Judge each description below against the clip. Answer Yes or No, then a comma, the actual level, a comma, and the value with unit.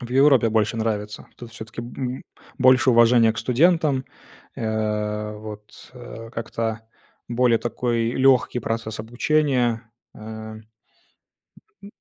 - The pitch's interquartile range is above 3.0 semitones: No, narrow, 2.4 semitones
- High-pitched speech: No, low, 115 Hz